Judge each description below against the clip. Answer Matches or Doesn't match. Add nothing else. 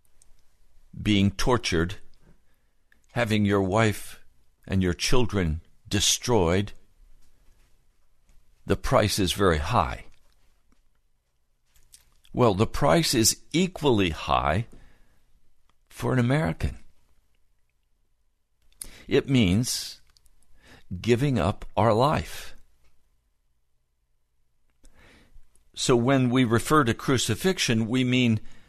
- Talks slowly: Matches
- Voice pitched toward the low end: Matches